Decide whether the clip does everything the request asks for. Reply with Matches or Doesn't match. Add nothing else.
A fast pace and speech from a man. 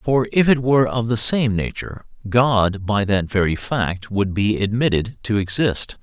Doesn't match